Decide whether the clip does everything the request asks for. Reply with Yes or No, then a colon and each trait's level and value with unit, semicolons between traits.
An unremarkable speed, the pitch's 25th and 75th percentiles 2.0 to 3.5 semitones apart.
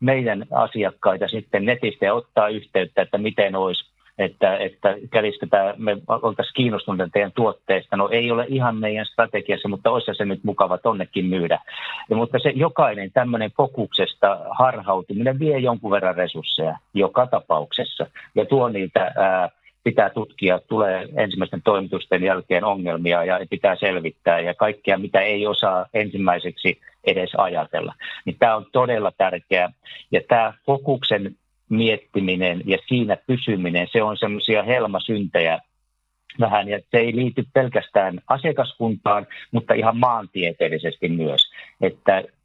No: average, 130 wpm; average, 3.9 semitones